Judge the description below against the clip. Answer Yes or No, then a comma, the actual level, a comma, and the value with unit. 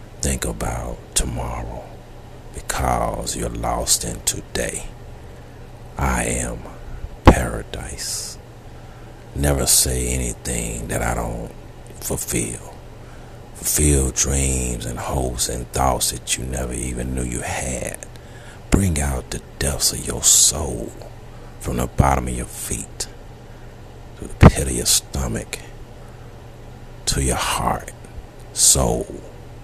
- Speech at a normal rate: No, slow, 110 wpm